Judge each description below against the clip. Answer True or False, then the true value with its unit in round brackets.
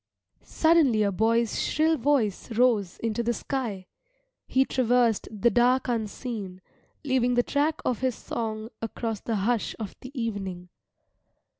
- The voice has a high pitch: True (235 Hz)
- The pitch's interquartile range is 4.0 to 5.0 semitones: False (3.0 semitones)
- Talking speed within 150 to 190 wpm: False (135 wpm)